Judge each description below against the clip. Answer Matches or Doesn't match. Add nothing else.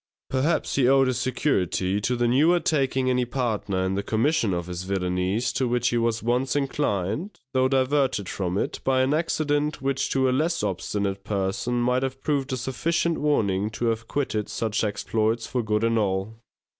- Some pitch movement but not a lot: Matches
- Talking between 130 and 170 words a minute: Doesn't match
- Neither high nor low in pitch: Doesn't match